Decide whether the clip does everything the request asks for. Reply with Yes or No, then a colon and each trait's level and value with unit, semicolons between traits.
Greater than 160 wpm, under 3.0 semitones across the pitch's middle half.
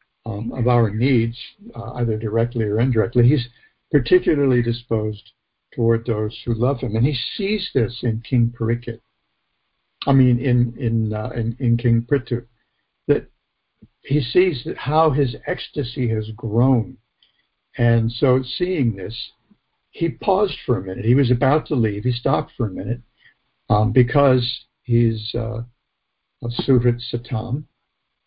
No: average, 140 wpm; narrow, 2.5 semitones